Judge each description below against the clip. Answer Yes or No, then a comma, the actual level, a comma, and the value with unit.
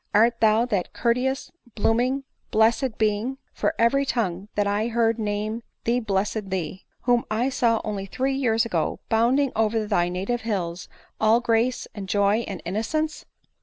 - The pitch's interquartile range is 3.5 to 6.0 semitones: No, average, 2.8 semitones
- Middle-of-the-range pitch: No, high, 225 Hz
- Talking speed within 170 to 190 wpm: No, average, 155 wpm